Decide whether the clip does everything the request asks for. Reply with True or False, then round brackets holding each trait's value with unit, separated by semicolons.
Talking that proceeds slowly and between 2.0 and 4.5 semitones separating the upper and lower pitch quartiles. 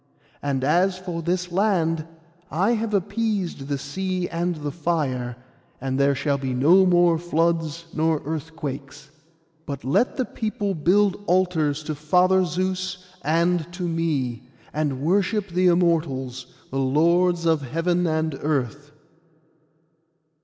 True (130 wpm; 3.9 semitones)